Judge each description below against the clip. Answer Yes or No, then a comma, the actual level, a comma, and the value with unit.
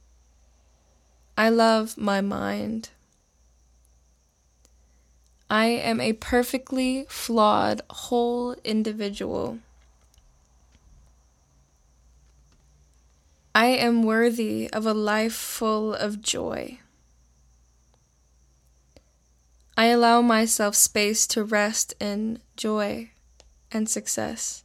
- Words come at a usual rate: No, slow, 75 wpm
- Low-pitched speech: Yes, very low, 85 Hz